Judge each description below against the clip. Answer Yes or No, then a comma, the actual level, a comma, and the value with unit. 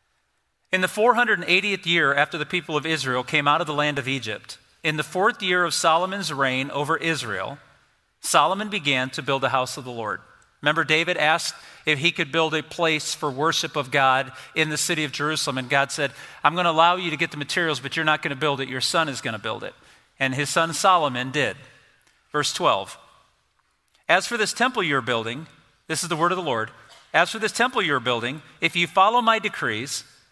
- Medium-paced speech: No, fast, 215 wpm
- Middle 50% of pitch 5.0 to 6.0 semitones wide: No, average, 3.4 semitones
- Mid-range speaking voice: Yes, medium, 155 Hz